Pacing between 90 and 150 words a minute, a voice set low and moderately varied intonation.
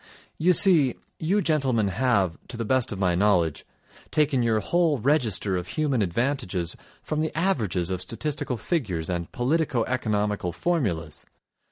No: average, 145 wpm; low, 120 Hz; wide, 8.2 semitones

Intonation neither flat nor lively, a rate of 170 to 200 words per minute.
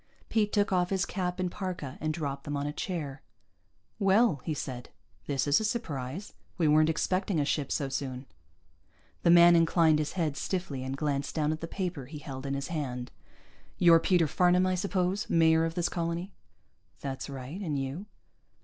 Yes: average, 4.3 semitones; average, 185 wpm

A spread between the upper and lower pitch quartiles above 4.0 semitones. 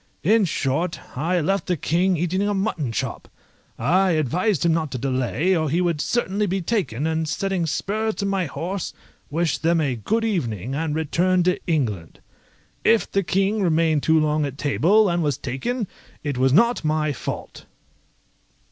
Yes: average, 4.7 semitones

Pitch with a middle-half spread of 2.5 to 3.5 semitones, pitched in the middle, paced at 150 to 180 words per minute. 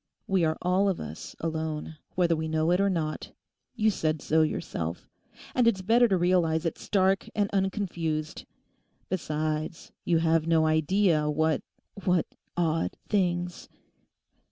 No: average, 3.2 semitones; medium, 165 Hz; slow, 135 wpm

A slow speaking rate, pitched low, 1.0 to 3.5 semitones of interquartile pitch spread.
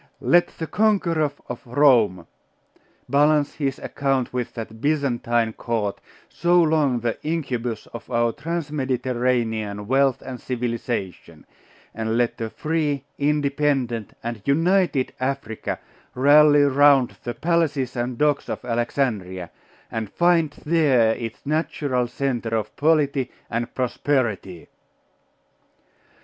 No: slow, 115 wpm; low, 130 Hz; average, 4.1 semitones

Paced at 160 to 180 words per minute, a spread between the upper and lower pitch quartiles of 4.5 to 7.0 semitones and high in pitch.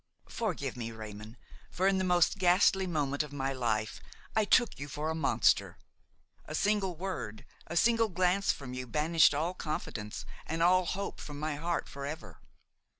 No: average, 165 wpm; average, 5.2 semitones; medium, 160 Hz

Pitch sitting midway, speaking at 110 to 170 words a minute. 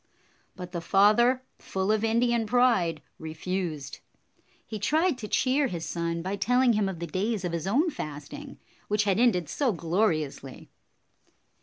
No: high, 200 Hz; average, 150 wpm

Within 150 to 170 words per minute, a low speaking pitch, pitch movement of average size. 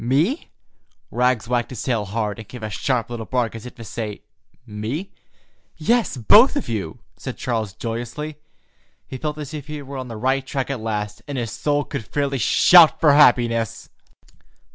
No: average, 180 wpm; low, 125 Hz; average, 4.3 semitones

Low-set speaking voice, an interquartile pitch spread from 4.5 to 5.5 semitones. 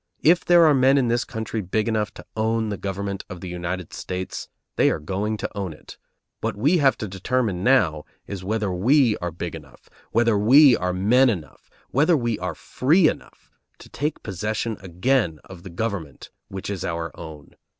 Yes: low, 105 Hz; average, 5.2 semitones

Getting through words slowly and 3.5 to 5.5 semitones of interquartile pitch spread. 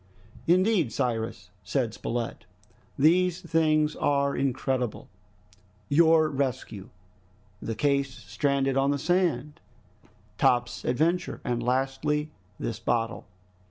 Yes: slow, 95 wpm; average, 4.1 semitones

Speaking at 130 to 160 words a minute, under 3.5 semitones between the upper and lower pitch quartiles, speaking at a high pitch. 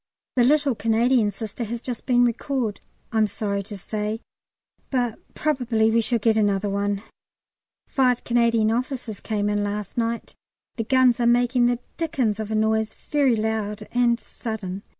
Yes: average, 155 wpm; narrow, 2.5 semitones; high, 225 Hz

